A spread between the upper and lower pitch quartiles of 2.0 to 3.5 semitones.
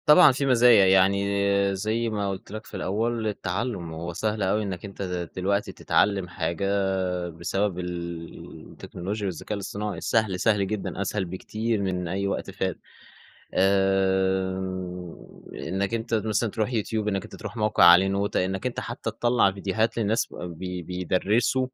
Yes: average, 2.7 semitones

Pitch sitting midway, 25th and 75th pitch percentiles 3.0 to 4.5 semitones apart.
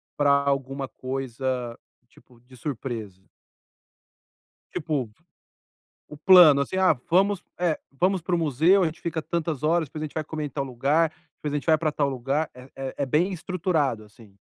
Yes: medium, 145 Hz; average, 3.7 semitones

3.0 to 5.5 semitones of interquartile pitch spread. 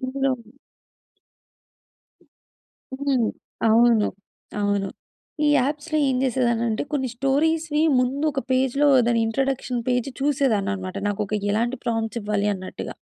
Yes: average, 3.7 semitones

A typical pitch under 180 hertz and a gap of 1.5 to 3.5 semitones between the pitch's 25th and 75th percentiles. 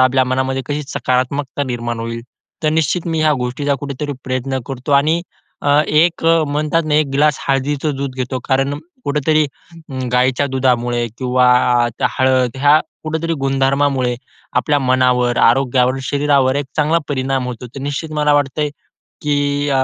Yes: low, 135 Hz; narrow, 2.4 semitones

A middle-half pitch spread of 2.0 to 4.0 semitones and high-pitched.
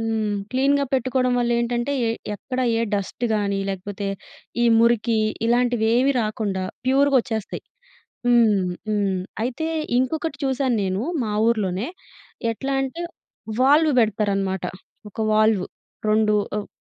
Yes: average, 3.7 semitones; high, 230 Hz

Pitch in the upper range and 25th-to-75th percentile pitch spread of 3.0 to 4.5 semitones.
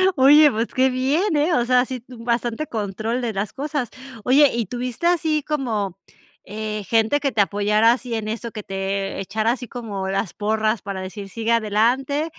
Yes: high, 230 Hz; average, 3.7 semitones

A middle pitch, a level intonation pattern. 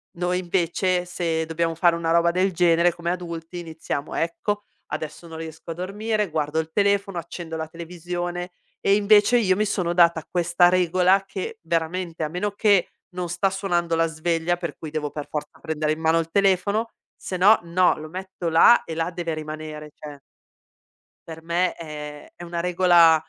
Yes: medium, 170 Hz; narrow, 2.2 semitones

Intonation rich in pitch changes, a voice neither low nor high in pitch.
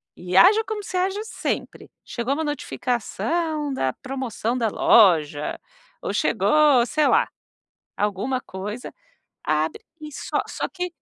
No: wide, 7.4 semitones; very high, 260 Hz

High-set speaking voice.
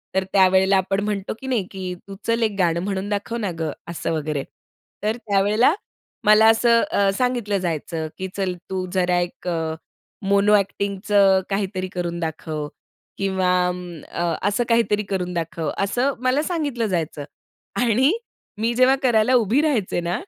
Yes: high, 195 Hz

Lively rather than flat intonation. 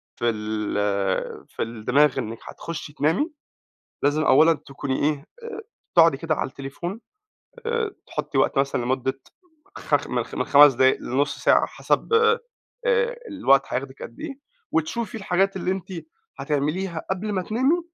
Yes: wide, 6.6 semitones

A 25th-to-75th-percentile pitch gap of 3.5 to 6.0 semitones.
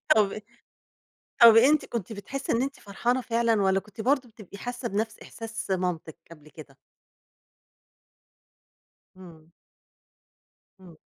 Yes: average, 4.1 semitones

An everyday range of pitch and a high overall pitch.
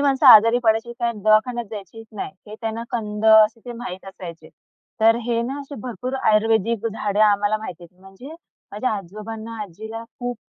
No: narrow, 2.1 semitones; high, 220 Hz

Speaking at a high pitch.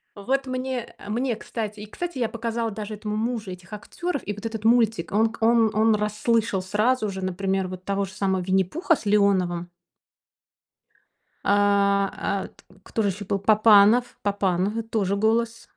Yes: high, 210 Hz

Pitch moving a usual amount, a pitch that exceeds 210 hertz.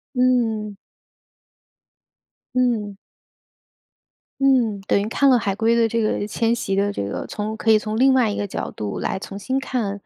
Yes: average, 3.2 semitones; high, 220 Hz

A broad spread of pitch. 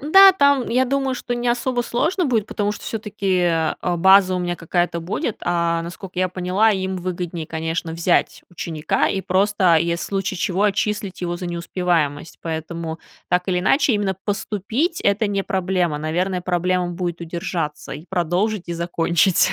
No: average, 3.3 semitones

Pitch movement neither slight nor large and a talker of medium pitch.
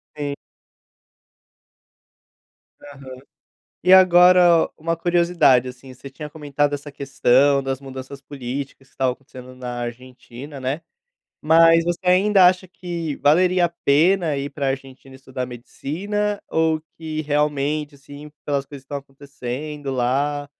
Yes: average, 3.7 semitones; medium, 145 Hz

